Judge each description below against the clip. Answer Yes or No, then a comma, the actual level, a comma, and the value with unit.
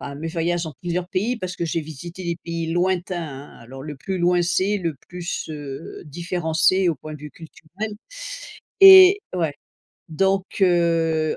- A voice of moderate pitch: Yes, medium, 170 Hz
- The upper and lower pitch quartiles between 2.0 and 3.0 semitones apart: Yes, narrow, 2.6 semitones